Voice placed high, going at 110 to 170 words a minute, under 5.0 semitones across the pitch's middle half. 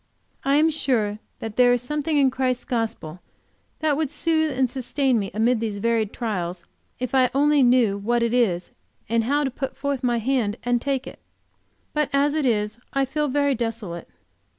No: very high, 250 Hz; average, 185 wpm; average, 3.7 semitones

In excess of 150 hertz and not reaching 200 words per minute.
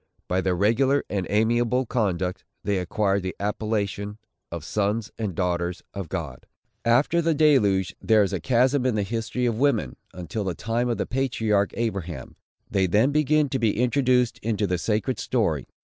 No: low, 105 Hz; average, 170 wpm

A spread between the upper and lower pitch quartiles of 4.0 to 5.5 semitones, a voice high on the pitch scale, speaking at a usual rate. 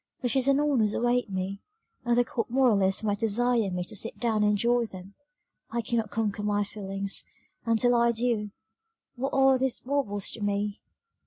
No: average, 3.1 semitones; high, 225 Hz; average, 175 wpm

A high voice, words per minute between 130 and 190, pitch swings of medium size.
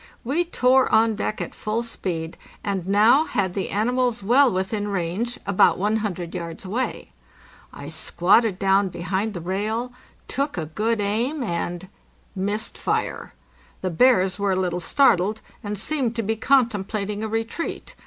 Yes: high, 205 Hz; average, 150 wpm; average, 3.7 semitones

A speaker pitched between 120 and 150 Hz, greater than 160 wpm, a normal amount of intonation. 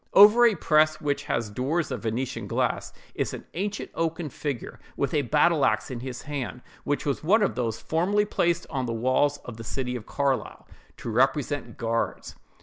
Yes: medium, 140 Hz; average, 185 wpm; average, 4.7 semitones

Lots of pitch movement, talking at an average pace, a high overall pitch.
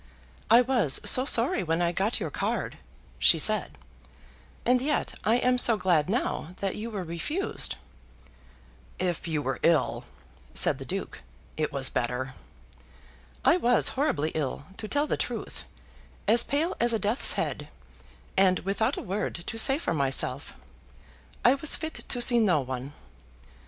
Yes: wide, 7.7 semitones; average, 155 wpm; high, 200 Hz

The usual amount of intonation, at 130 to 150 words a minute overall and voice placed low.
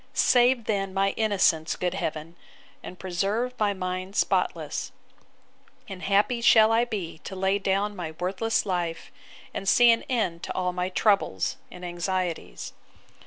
No: average, 3.0 semitones; average, 145 wpm; high, 190 Hz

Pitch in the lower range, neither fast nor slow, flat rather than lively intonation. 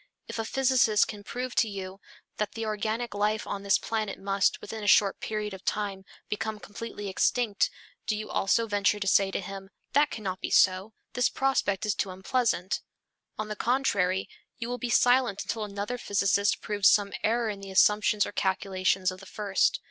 No: high, 205 Hz; average, 185 wpm; narrow, 2.3 semitones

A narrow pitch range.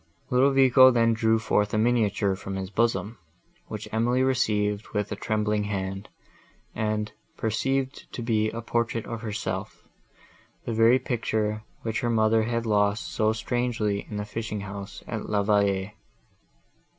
Yes: narrow, 2.1 semitones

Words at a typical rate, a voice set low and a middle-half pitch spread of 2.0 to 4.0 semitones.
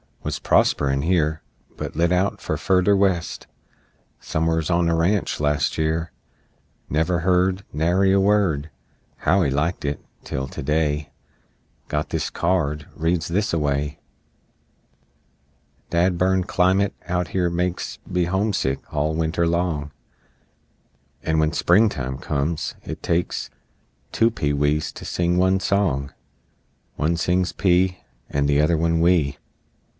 No: slow, 130 wpm; very low, 85 Hz; average, 3.4 semitones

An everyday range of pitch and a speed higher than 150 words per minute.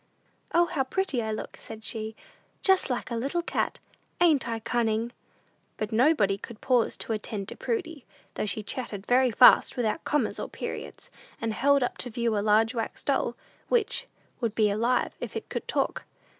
Yes: average, 3.9 semitones; average, 180 wpm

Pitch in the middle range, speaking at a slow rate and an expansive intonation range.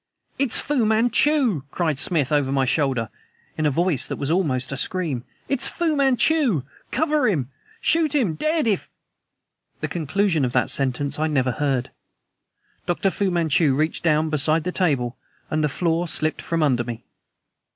No: medium, 160 Hz; average, 165 wpm; wide, 7.0 semitones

